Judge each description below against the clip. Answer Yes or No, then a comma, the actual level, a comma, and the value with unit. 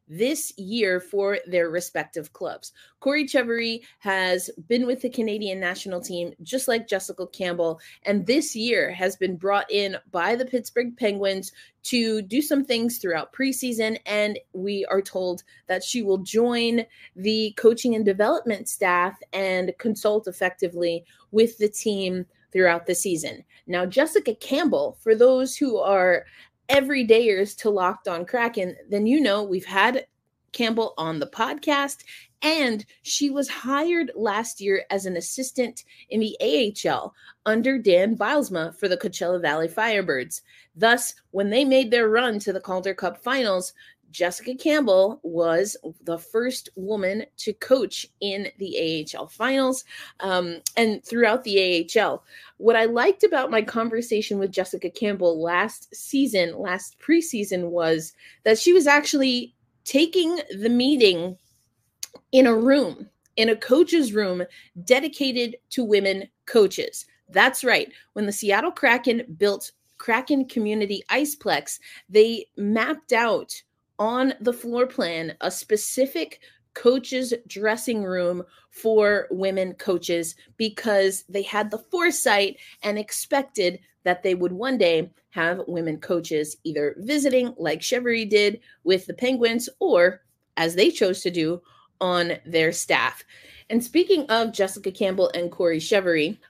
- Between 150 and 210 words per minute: No, average, 140 wpm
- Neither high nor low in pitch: No, high, 210 Hz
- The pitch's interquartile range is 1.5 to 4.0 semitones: No, average, 5.2 semitones